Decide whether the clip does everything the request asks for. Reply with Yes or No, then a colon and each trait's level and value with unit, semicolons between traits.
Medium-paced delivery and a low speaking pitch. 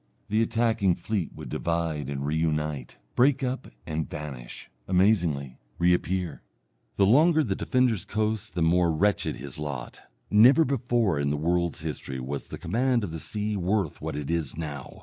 Yes: average, 165 wpm; very low, 85 Hz